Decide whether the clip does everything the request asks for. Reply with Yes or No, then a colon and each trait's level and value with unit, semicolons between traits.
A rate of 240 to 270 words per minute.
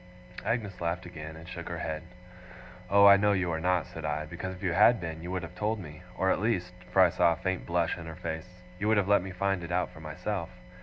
Yes: fast, 260 wpm